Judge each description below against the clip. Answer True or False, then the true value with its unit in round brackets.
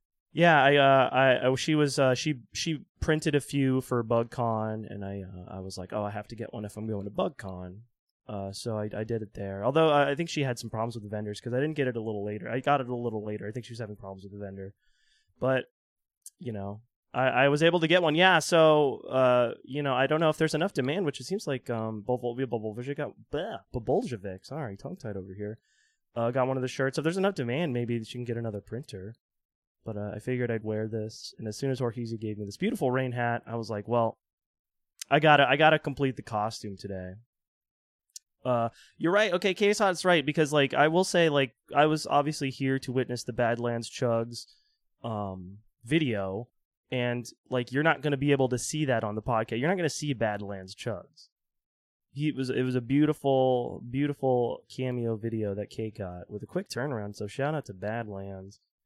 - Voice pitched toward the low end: True (125 Hz)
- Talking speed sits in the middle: False (225 wpm)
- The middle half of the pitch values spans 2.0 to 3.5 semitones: False (4.9 semitones)